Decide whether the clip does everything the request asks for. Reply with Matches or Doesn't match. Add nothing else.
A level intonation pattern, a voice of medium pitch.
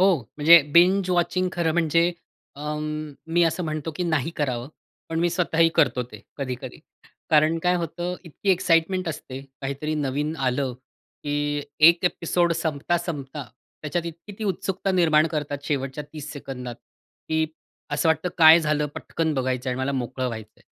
Doesn't match